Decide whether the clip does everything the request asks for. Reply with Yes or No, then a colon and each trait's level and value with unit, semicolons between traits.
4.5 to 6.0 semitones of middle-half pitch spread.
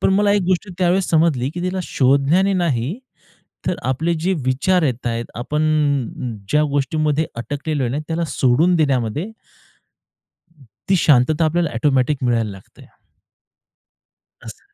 Yes: average, 5.1 semitones